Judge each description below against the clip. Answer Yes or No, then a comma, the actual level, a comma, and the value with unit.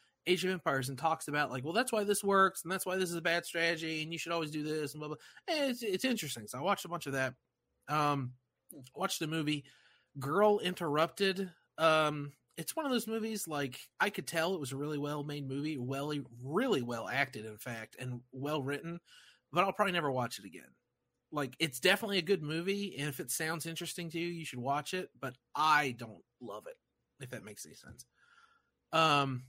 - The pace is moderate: No, fast, 220 wpm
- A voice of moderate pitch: Yes, medium, 160 Hz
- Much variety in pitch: No, average, 4.8 semitones